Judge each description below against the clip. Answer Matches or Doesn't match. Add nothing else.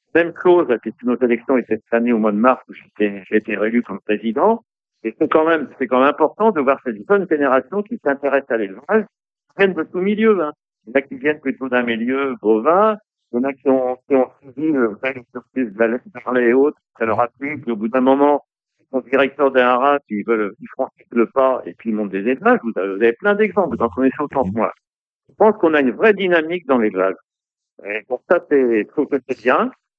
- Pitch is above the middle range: Doesn't match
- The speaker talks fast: Matches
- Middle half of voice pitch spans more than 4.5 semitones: Matches